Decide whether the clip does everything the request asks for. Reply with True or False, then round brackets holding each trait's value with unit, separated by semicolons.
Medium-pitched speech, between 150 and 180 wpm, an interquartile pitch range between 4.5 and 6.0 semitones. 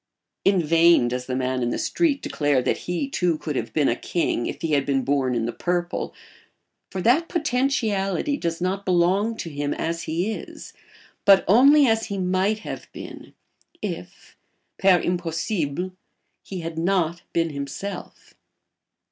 True (175 Hz; 160 wpm; 5.1 semitones)